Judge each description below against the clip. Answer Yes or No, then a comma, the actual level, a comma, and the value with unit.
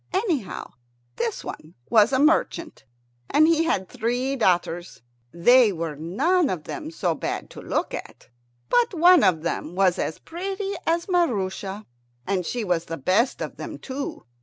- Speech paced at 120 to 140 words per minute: No, average, 160 wpm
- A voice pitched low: No, high, 235 Hz